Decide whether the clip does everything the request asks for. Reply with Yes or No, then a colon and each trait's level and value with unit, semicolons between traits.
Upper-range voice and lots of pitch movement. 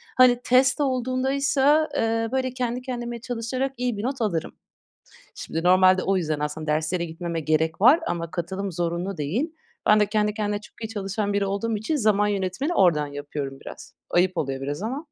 Yes: high, 205 Hz; wide, 6.5 semitones